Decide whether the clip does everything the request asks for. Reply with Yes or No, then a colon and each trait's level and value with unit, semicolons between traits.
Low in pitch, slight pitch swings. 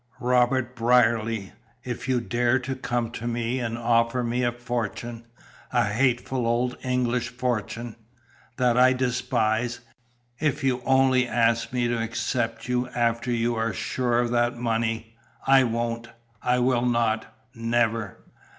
Yes: low, 120 Hz; narrow, 1.3 semitones